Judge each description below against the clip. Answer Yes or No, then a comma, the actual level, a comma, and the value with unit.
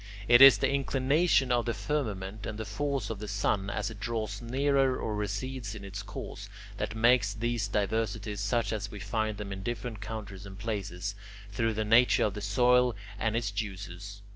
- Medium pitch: No, low, 110 Hz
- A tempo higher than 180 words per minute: Yes, average, 190 wpm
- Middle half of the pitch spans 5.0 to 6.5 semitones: No, average, 3.1 semitones